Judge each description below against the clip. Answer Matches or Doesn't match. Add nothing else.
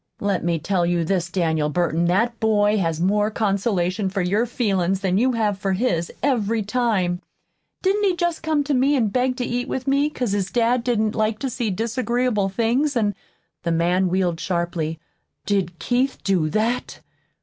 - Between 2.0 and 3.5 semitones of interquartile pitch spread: Doesn't match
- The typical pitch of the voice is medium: Doesn't match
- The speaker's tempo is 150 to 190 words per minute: Matches